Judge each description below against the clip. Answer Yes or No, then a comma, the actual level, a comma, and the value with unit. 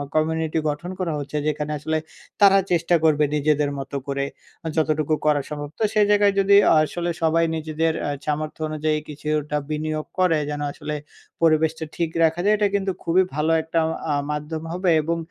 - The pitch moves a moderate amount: No, narrow, 1.8 semitones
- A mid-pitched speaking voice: Yes, medium, 155 Hz